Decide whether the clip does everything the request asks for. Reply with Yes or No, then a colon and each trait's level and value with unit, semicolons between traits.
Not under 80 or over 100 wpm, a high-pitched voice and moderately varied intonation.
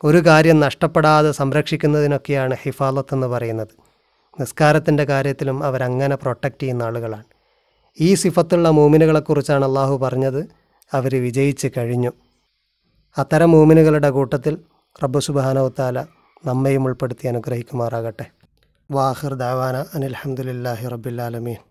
No: average, 90 wpm; low, 135 Hz; average, 3.2 semitones